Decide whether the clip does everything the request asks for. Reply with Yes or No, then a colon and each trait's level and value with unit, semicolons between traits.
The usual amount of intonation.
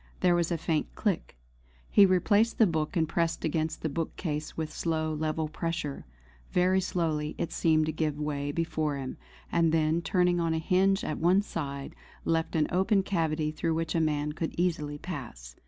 No: narrow, 2.3 semitones